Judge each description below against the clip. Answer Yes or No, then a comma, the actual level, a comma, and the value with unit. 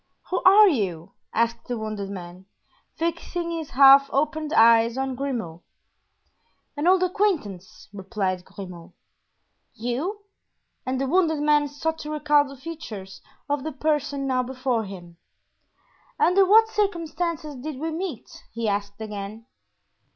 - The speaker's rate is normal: No, slow, 130 wpm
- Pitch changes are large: Yes, wide, 6.8 semitones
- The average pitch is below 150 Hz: No, very high, 270 Hz